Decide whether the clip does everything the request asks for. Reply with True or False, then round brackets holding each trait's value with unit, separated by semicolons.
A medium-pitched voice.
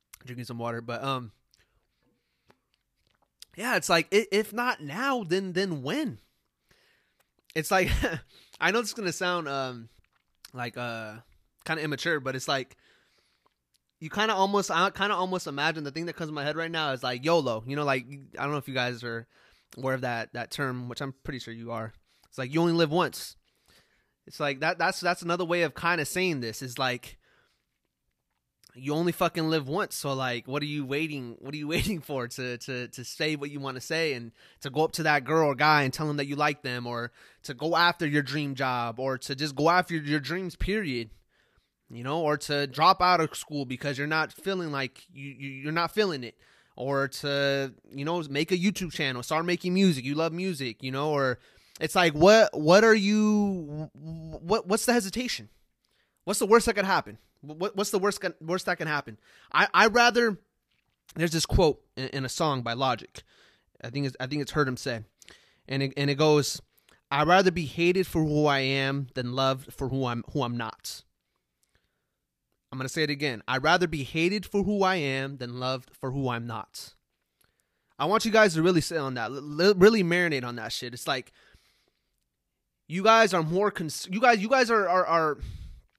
True (150 Hz)